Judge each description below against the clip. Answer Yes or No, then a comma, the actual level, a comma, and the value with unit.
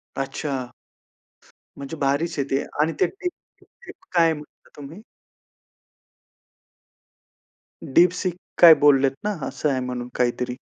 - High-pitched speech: No, medium, 145 Hz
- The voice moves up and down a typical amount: Yes, average, 3.8 semitones